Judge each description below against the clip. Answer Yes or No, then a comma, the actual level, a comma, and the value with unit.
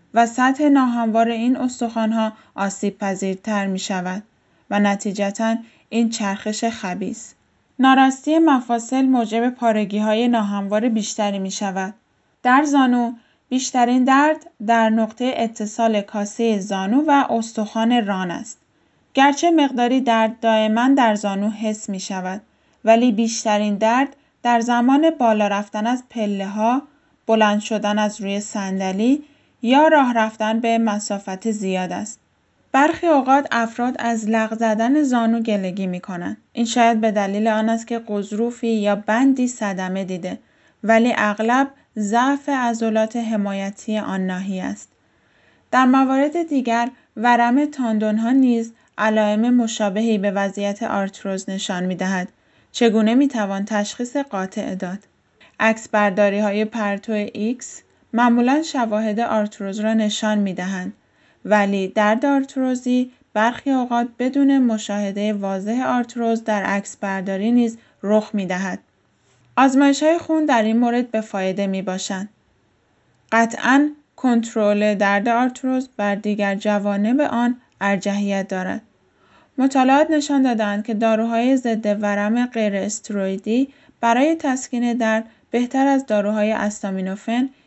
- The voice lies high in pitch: Yes, high, 225 Hz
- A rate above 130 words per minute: No, average, 125 wpm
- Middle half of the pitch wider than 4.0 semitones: No, average, 3.3 semitones